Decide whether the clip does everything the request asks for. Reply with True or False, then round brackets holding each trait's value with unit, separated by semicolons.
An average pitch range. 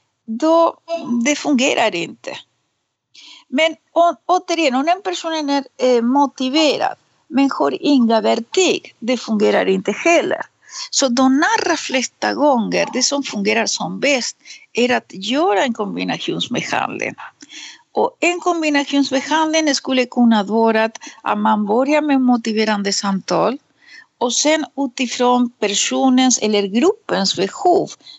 False (5.7 semitones)